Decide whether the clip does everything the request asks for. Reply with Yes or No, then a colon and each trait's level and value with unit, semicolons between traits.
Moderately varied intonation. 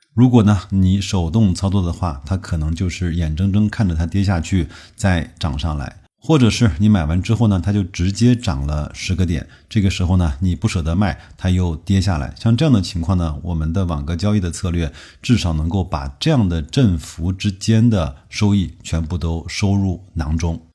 Yes: average, 3.8 semitones